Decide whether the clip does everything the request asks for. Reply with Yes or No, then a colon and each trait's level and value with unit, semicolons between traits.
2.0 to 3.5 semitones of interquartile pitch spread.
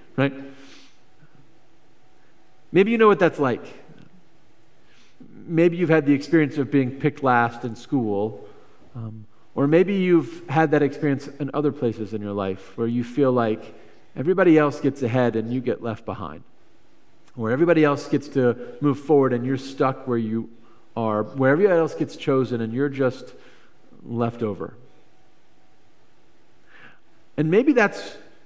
No: average, 4.3 semitones